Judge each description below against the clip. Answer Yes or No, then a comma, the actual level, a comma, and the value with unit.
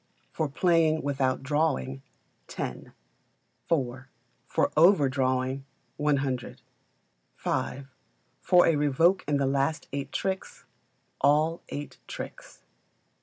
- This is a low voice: No, medium, 145 Hz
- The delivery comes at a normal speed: No, slow, 100 wpm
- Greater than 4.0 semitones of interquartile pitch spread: No, average, 3.1 semitones